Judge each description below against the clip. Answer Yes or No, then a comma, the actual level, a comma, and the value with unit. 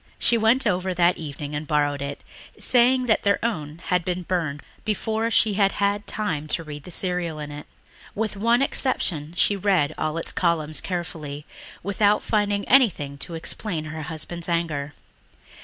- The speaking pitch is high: No, medium, 175 Hz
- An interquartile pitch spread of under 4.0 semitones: No, average, 5.2 semitones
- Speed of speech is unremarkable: Yes, average, 165 wpm